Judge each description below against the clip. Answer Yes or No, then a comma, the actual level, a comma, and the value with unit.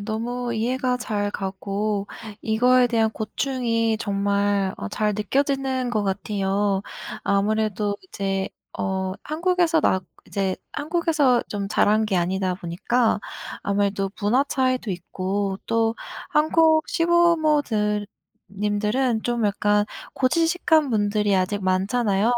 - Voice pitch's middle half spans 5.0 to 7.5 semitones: No, average, 4.2 semitones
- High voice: Yes, high, 215 Hz